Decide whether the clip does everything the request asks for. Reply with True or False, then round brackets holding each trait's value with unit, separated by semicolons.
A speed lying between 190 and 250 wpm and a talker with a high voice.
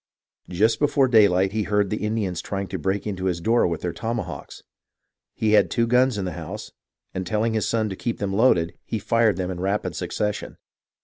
False (200 wpm; 105 Hz)